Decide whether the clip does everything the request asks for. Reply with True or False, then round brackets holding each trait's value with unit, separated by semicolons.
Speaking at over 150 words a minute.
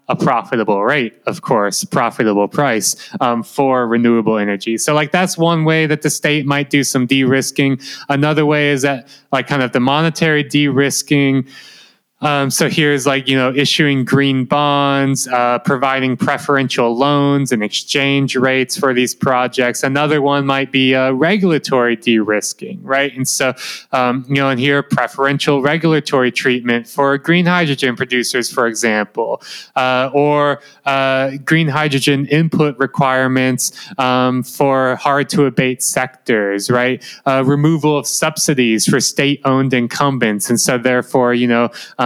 False (145 wpm)